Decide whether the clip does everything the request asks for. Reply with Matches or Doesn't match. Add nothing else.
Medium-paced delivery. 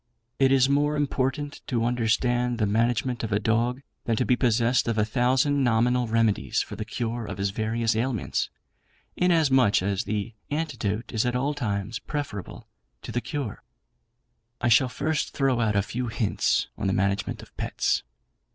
Matches